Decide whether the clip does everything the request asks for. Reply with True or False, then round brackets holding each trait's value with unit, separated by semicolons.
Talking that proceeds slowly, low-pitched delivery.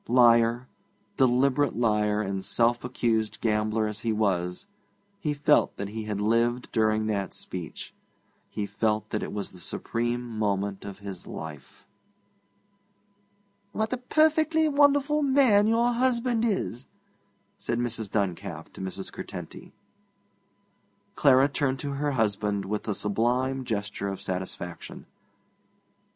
True (125 wpm; 115 Hz)